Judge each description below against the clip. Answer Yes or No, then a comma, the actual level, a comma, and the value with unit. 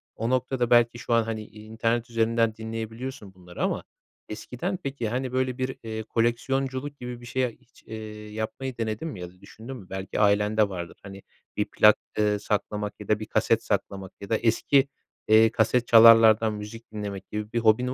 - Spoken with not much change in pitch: Yes, narrow, 2.3 semitones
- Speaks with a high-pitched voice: No, low, 110 Hz